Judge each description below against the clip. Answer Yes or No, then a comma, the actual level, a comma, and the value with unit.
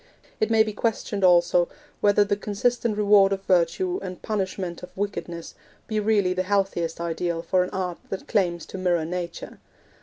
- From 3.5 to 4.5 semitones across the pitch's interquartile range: No, average, 2.9 semitones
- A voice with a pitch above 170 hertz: Yes, high, 190 Hz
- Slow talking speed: No, average, 170 wpm